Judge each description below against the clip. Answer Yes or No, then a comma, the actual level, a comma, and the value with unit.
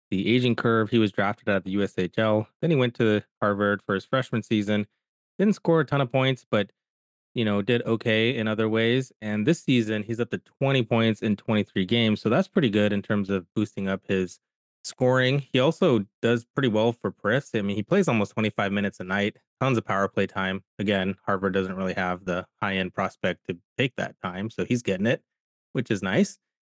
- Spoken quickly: Yes, fast, 215 wpm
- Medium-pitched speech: No, low, 110 Hz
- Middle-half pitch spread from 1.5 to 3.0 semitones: No, average, 3.4 semitones